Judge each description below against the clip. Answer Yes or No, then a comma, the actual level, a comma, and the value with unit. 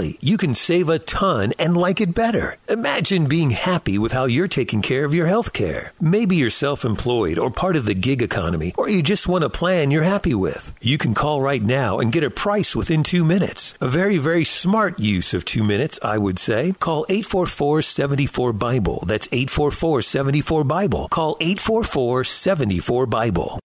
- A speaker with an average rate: Yes, average, 190 wpm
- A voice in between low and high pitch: Yes, medium, 155 Hz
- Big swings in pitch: Yes, wide, 6.4 semitones